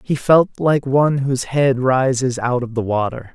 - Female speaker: No, male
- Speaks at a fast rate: No, average, 195 wpm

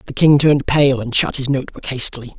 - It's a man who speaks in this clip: Yes, male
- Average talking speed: No, fast, 250 wpm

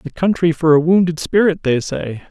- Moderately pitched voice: Yes, medium, 165 Hz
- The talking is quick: Yes, fast, 210 wpm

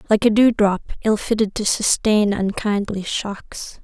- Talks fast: No, average, 155 wpm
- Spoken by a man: No, female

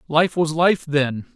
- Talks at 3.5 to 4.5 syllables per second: Yes, 3.6 syllables/s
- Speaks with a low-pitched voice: No, medium, 155 Hz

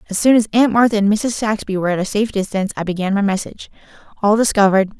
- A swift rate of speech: Yes, fast, 230 wpm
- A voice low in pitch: No, high, 205 Hz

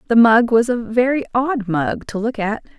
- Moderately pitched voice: No, high, 230 Hz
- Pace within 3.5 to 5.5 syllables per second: Yes, 4.6 syllables/s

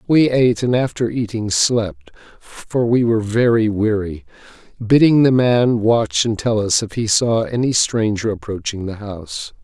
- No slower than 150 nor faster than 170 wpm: Yes, average, 160 wpm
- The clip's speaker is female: No, male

